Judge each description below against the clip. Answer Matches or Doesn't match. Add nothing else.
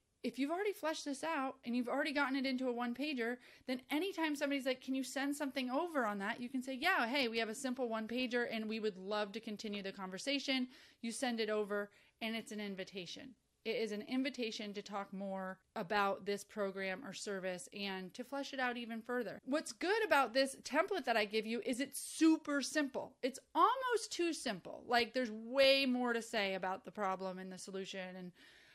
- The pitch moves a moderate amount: Matches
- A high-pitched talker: Matches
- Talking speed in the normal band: Doesn't match